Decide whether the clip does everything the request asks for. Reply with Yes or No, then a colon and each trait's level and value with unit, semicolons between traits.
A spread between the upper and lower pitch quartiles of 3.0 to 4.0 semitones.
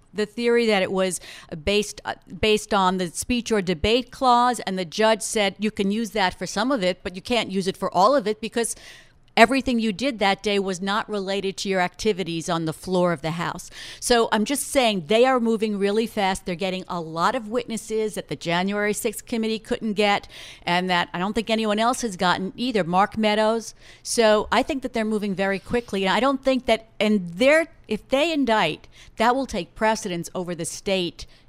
Yes: average, 3.5 semitones